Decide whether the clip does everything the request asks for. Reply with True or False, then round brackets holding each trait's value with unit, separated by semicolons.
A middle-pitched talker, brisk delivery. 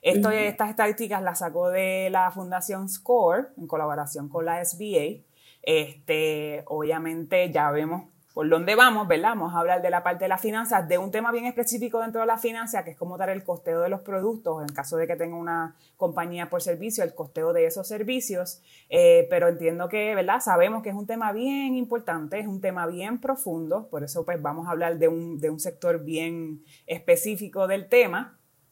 True (180 Hz; 200 wpm)